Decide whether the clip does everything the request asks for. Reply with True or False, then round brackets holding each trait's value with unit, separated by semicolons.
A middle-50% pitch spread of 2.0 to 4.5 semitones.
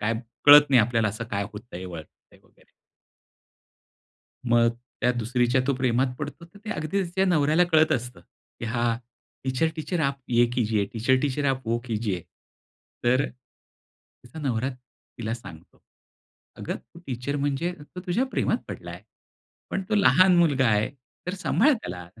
False (5.1 semitones)